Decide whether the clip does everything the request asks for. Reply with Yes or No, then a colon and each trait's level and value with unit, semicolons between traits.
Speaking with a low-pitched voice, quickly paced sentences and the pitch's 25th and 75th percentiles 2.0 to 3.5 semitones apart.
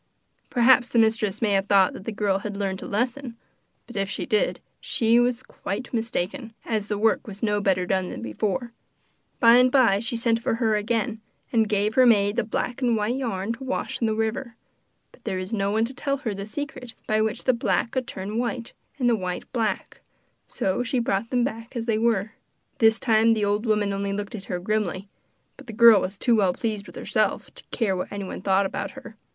No: high, 220 Hz; fast, 220 wpm; average, 2.9 semitones